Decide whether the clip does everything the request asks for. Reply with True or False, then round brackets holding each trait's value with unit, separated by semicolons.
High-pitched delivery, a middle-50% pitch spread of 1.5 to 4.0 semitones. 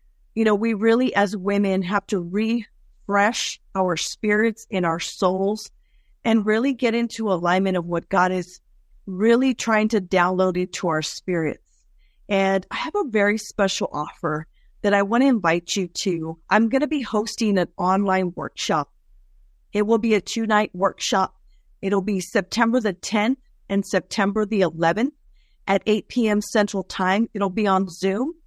True (200 Hz; 3.0 semitones)